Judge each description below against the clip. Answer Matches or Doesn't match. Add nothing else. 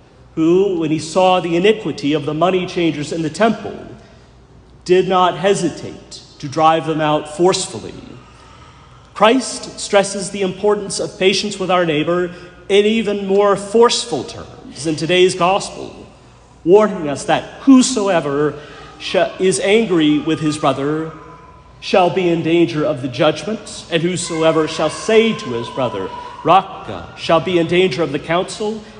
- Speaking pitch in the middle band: Matches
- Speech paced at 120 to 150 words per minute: Matches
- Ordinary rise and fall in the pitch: Matches